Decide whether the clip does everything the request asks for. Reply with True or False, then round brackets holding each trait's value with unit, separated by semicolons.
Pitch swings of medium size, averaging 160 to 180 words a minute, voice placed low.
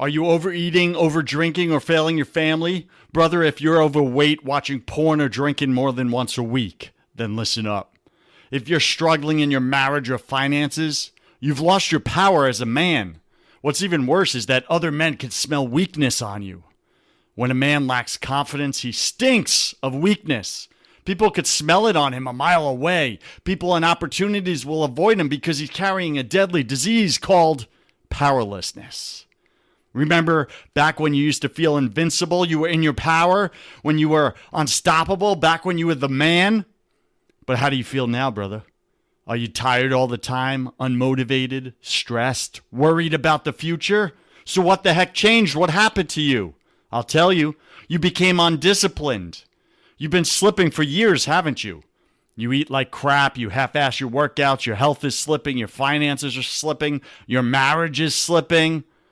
False (4.3 semitones; 170 wpm; 150 Hz)